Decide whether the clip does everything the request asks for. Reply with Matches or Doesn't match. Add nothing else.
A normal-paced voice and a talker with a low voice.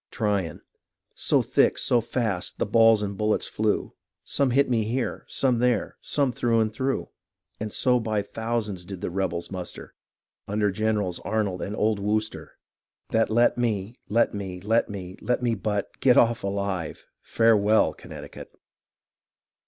Matches